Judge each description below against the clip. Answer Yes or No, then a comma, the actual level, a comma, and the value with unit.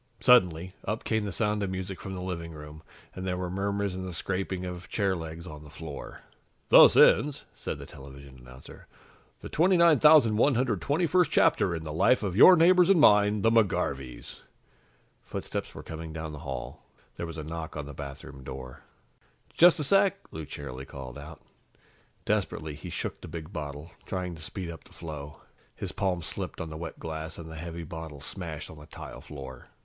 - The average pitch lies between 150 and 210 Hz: No, very low, 85 Hz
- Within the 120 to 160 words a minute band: No, average, 185 wpm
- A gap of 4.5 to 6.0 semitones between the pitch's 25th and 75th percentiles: Yes, average, 5.1 semitones